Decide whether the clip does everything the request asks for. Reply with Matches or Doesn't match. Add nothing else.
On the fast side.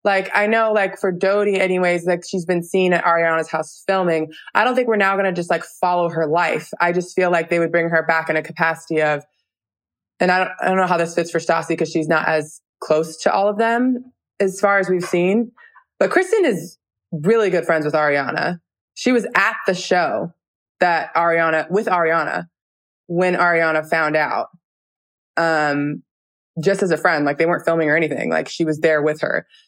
Matches